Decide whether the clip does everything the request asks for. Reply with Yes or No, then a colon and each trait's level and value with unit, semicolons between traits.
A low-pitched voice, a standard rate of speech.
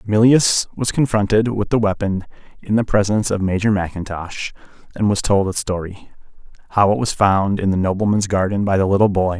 Yes: low, 100 Hz; average, 180 wpm